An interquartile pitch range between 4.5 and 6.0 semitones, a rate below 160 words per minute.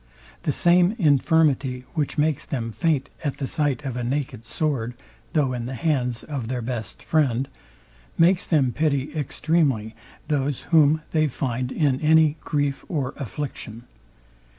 No: average, 3.6 semitones; average, 145 wpm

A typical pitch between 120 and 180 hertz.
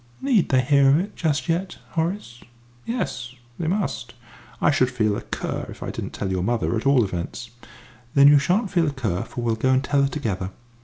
Yes: low, 135 Hz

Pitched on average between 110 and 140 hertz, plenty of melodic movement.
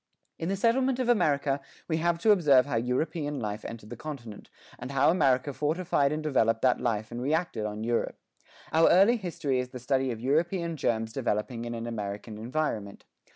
Yes: low, 135 Hz; wide, 5.8 semitones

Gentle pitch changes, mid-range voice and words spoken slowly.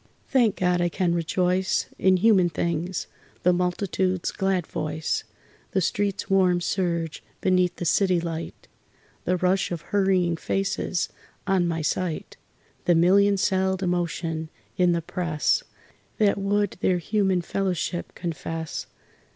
Yes: narrow, 2.0 semitones; medium, 180 Hz; slow, 125 wpm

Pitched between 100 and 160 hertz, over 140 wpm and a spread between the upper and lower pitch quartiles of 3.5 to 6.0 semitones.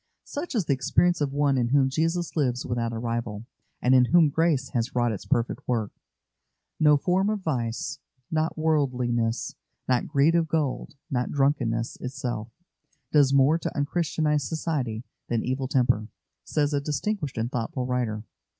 Yes: low, 135 Hz; average, 160 wpm; average, 4.3 semitones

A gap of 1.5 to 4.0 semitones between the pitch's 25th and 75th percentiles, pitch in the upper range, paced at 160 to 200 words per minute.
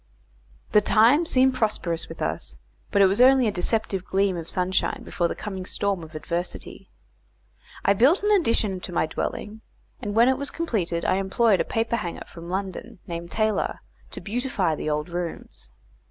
No: average, 4.8 semitones; high, 195 Hz; average, 170 wpm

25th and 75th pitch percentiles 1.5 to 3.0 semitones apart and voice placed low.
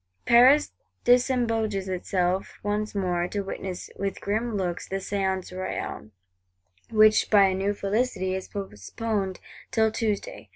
No: average, 2.7 semitones; high, 200 Hz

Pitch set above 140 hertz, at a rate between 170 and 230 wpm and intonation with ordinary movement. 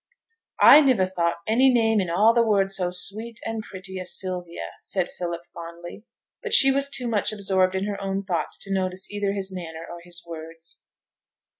Yes: high, 190 Hz; average, 185 wpm; average, 3.6 semitones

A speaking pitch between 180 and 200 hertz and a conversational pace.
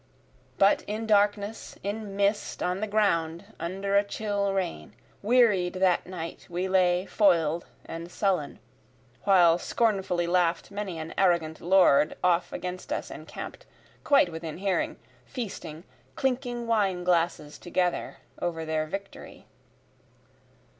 No: medium, 185 Hz; slow, 120 wpm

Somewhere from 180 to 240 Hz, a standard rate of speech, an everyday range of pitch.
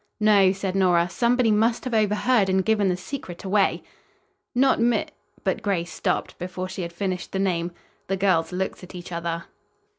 Yes: high, 190 Hz; average, 180 wpm; average, 3.0 semitones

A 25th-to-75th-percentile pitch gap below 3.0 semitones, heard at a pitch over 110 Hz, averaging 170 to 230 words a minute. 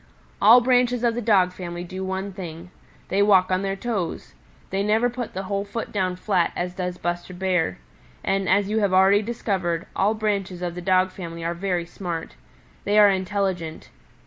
Yes: narrow, 2.4 semitones; high, 190 Hz; average, 185 wpm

